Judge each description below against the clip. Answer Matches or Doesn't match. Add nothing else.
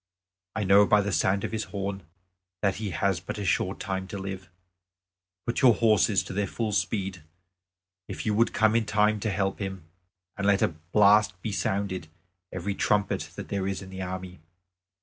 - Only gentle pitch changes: Matches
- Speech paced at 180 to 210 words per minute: Matches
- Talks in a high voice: Doesn't match